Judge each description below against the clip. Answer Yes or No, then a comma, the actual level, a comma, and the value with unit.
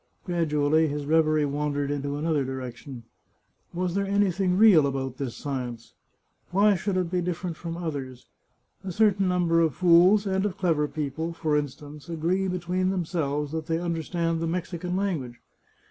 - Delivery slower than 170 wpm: Yes, average, 155 wpm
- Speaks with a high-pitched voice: No, medium, 165 Hz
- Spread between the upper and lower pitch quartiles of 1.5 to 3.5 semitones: No, average, 3.9 semitones